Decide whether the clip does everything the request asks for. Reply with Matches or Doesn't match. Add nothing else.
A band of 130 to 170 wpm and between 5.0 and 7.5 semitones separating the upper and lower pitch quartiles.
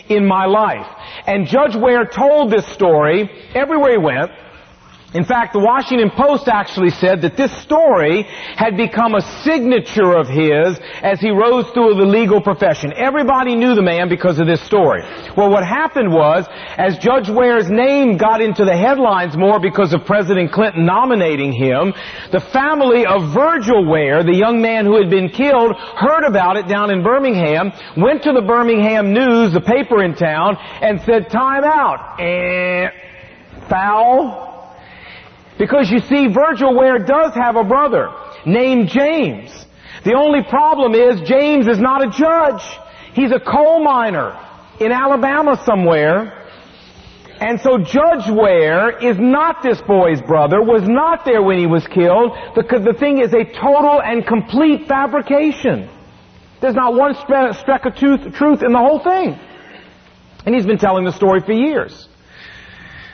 Matches